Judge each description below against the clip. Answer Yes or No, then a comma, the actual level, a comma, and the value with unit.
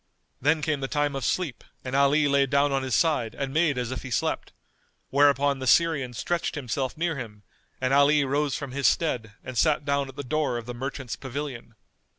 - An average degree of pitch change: No, narrow, 2.3 semitones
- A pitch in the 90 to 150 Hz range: Yes, medium, 140 Hz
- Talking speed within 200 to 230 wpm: Yes, fast, 205 wpm